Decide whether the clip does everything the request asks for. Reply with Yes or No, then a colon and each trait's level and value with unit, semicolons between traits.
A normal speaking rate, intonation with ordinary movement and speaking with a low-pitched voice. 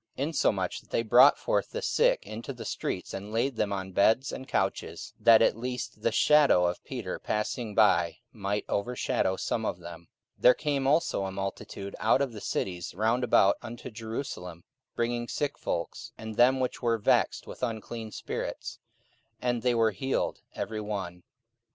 Yes: average, 175 wpm; average, 3.9 semitones; low, 110 Hz